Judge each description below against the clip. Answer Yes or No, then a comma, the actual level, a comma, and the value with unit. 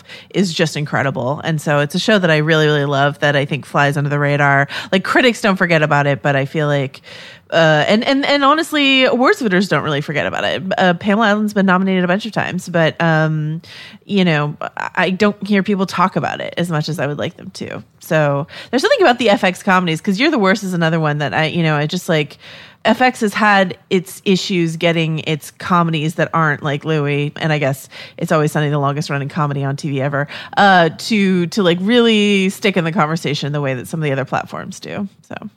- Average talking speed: No, fast, 230 wpm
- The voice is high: No, medium, 165 Hz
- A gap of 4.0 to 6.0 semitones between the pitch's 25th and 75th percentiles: Yes, average, 4.7 semitones